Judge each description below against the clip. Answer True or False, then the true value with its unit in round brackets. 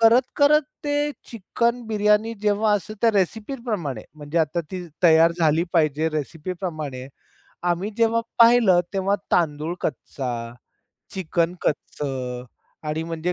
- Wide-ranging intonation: True (6.1 semitones)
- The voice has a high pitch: False (180 Hz)